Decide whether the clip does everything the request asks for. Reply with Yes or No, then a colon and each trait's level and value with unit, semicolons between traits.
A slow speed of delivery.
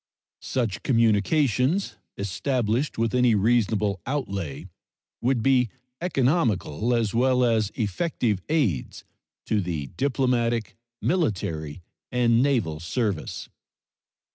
Yes: slow, 90 wpm